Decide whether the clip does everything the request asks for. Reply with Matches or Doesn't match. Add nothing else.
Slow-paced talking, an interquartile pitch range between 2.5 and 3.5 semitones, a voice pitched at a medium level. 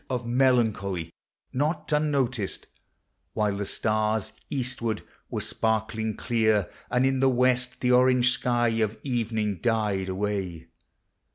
Doesn't match